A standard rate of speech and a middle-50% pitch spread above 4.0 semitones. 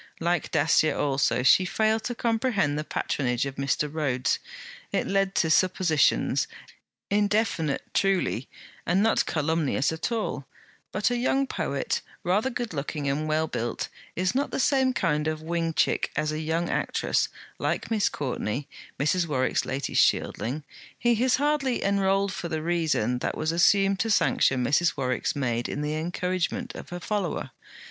Yes: average, 155 wpm; wide, 5.4 semitones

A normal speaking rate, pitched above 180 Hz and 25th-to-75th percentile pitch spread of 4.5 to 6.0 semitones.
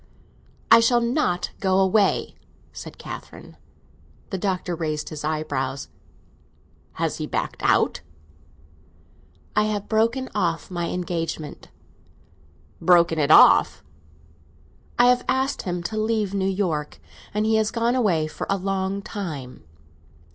No: slow, 125 wpm; high, 190 Hz; average, 4.8 semitones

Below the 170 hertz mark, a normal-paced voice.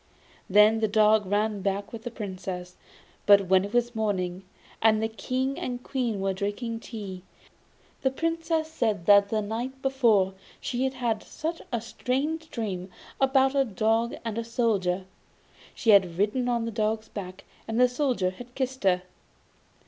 No: high, 220 Hz; average, 165 wpm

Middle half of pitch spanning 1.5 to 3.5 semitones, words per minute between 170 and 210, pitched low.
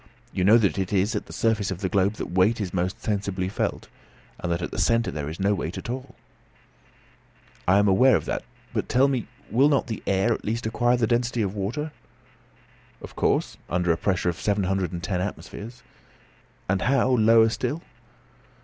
No: average, 4.0 semitones; average, 200 wpm; low, 105 Hz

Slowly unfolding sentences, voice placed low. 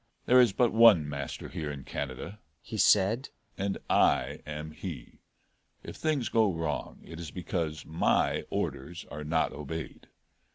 No: average, 150 wpm; very low, 85 Hz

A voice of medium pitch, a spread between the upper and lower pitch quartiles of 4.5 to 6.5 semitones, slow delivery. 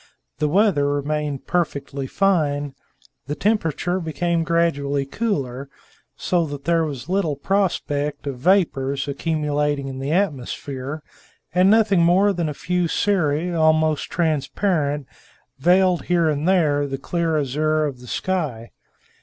No: medium, 155 Hz; average, 3.8 semitones; slow, 130 wpm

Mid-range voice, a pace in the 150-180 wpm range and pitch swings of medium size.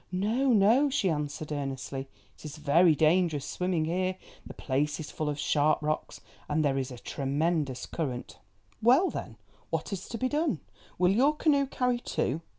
No: medium, 160 Hz; average, 170 wpm; wide, 6.8 semitones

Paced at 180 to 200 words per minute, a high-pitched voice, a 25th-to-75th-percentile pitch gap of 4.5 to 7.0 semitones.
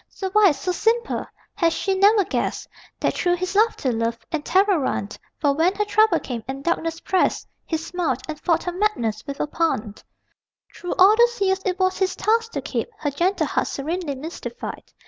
Yes: average, 190 wpm; very high, 355 Hz; average, 5.2 semitones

